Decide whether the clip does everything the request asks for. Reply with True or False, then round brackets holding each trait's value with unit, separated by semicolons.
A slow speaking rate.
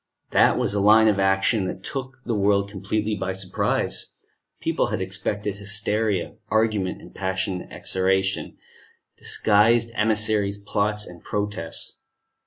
True (125 wpm)